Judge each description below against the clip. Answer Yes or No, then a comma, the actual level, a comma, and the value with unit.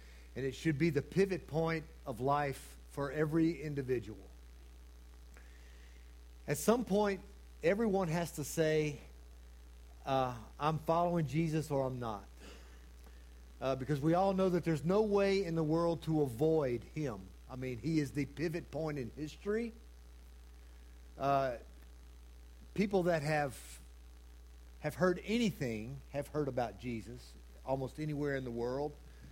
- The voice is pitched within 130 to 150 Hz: Yes, low, 135 Hz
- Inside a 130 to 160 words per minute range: Yes, slow, 135 wpm